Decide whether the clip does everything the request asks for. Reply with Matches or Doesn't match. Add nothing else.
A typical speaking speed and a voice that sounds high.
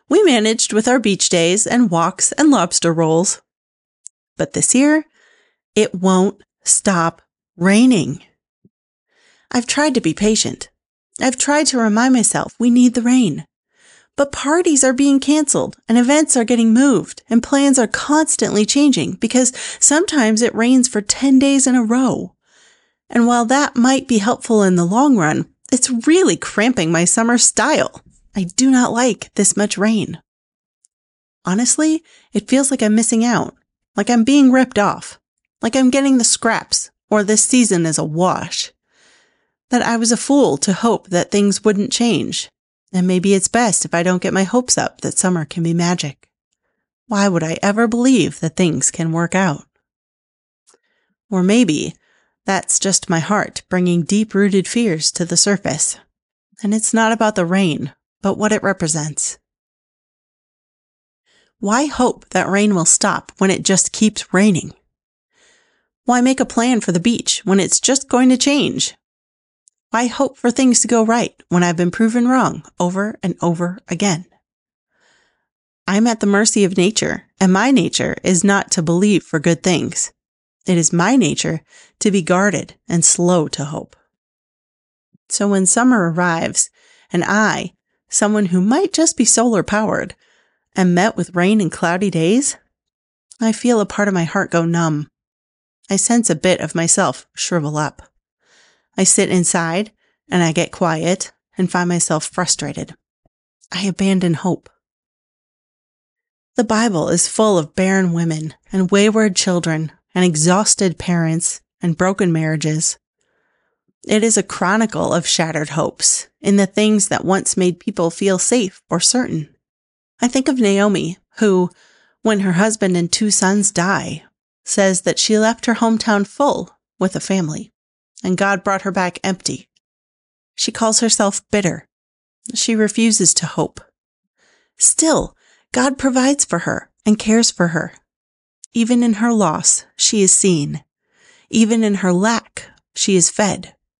Matches